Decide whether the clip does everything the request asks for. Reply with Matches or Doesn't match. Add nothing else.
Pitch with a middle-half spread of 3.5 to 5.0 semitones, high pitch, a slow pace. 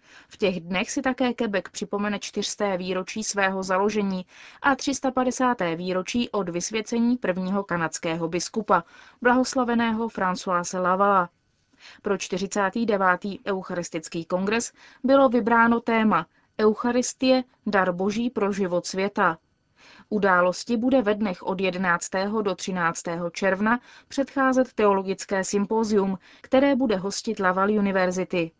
Matches